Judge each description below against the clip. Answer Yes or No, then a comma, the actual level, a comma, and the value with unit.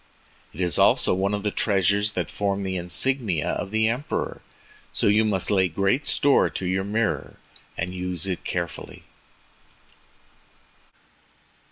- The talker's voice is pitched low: Yes, low, 100 Hz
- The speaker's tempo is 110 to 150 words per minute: Yes, average, 140 wpm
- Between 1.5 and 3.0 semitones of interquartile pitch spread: Yes, narrow, 2.6 semitones